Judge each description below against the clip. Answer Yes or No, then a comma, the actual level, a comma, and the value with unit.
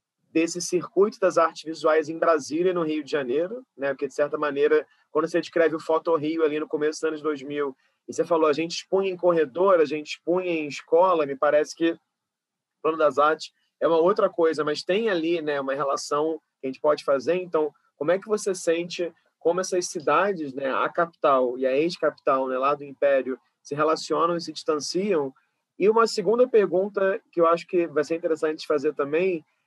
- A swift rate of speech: Yes, fast, 200 wpm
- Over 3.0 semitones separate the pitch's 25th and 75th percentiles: No, average, 2.7 semitones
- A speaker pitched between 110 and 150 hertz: No, medium, 160 Hz